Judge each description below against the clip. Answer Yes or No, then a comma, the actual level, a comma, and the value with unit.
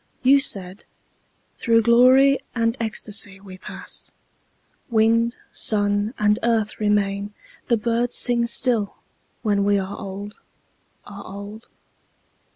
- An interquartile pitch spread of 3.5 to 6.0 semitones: No, narrow, 2.5 semitones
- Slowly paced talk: Yes, slow, 110 wpm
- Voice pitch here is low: No, high, 215 Hz